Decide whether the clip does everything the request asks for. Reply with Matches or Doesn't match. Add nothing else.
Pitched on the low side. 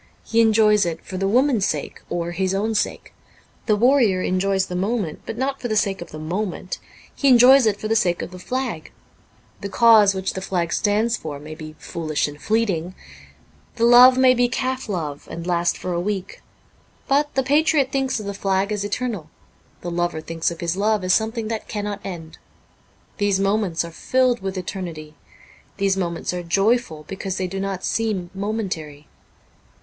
Doesn't match